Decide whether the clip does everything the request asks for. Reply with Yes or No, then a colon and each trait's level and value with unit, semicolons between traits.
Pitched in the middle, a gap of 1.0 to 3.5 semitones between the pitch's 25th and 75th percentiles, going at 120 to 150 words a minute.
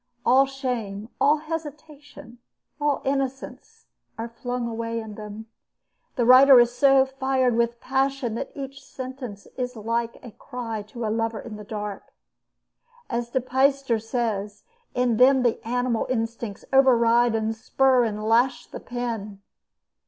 No: high, 240 Hz; average, 2.9 semitones; average, 140 wpm